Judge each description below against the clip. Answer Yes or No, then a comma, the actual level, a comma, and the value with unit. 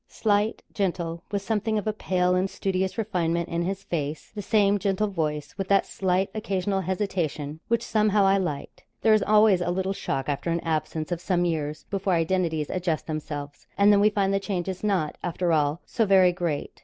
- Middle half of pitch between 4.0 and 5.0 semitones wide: No, average, 3.3 semitones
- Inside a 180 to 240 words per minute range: Yes, average, 195 wpm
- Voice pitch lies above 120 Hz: Yes, medium, 185 Hz